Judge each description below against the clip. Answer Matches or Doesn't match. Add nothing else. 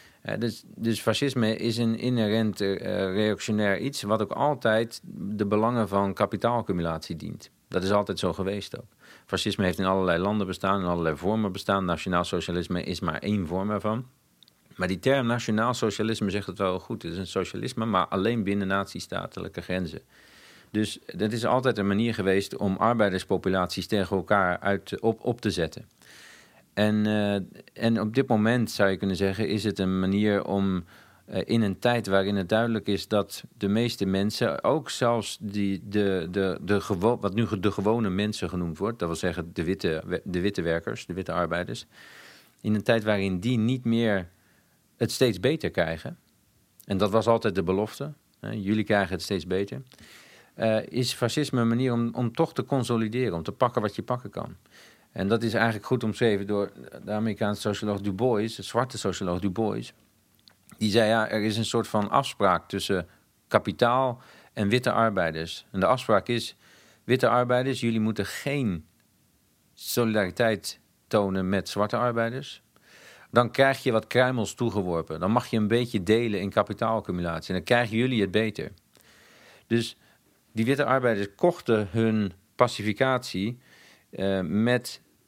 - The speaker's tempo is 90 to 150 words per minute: Doesn't match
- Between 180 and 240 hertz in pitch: Doesn't match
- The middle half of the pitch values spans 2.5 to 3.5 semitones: Matches